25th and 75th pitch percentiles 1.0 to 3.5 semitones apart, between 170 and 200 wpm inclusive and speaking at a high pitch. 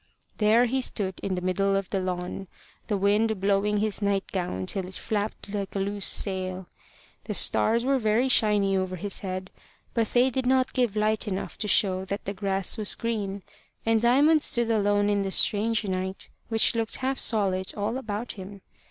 Yes: narrow, 2.6 semitones; average, 185 wpm; high, 205 Hz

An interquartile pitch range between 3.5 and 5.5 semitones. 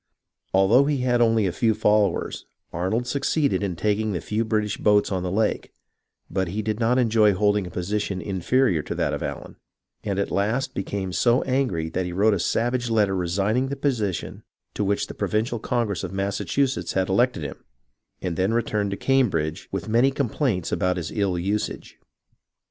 Yes: average, 3.8 semitones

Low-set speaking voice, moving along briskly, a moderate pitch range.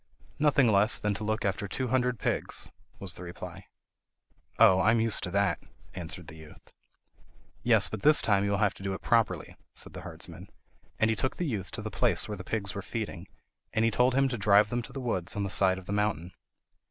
Yes: low, 105 Hz; fast, 225 wpm; average, 3.1 semitones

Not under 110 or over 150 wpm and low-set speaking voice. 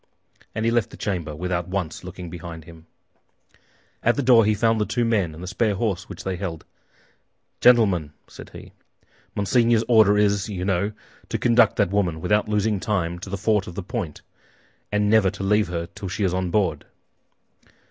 No: average, 180 wpm; low, 100 Hz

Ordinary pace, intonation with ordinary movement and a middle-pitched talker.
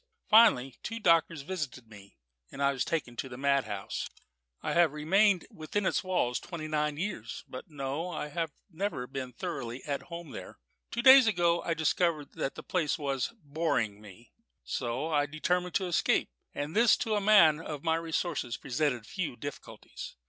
Yes: average, 170 wpm; average, 4.5 semitones; medium, 155 Hz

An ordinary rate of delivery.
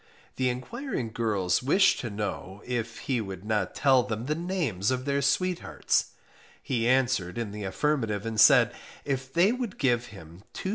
Yes: average, 160 wpm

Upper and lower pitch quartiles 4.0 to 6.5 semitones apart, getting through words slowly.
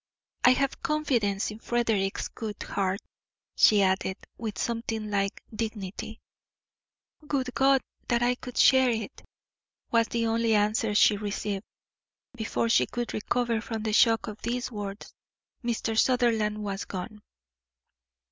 No: narrow, 2.5 semitones; slow, 130 wpm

